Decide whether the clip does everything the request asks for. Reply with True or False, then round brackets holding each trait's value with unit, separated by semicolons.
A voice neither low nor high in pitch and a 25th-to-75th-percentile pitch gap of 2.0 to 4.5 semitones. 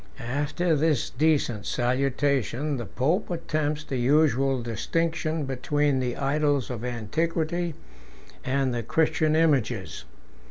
True (145 Hz; 3.7 semitones)